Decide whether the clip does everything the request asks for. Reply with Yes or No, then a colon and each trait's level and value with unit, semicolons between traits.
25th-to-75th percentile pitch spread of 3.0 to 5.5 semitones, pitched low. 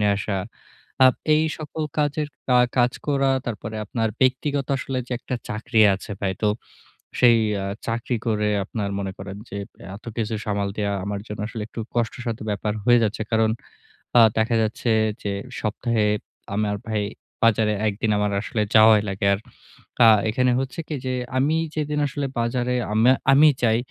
Yes: average, 3.3 semitones; low, 115 Hz